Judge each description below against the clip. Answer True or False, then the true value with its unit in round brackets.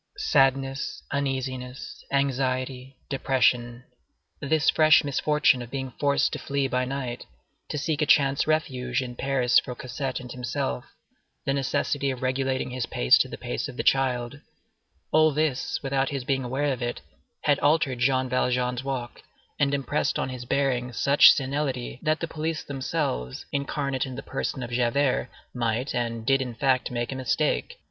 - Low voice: True (130 Hz)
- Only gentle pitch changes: True (2.0 semitones)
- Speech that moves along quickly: False (160 wpm)